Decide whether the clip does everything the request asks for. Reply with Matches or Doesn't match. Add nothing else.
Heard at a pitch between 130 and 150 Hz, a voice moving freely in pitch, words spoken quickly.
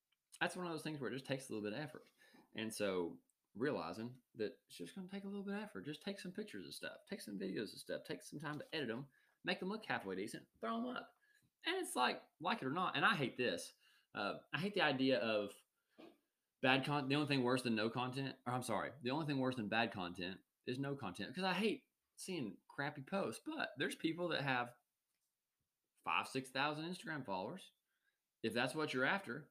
Matches